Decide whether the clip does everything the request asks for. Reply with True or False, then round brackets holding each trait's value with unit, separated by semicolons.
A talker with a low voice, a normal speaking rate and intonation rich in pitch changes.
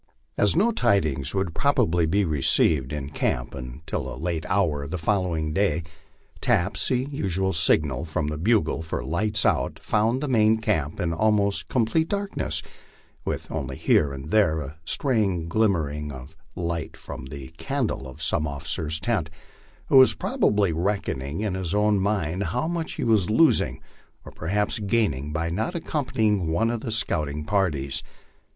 True (90 Hz; 165 wpm; 5.9 semitones)